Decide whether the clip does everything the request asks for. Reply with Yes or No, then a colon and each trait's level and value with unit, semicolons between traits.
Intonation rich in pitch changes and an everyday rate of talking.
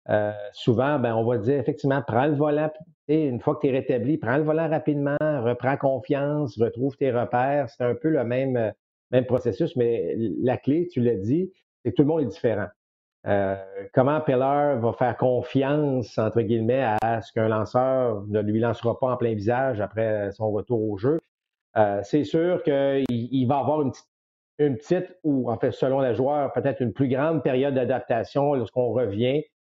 No: average, 3.9 semitones; average, 190 wpm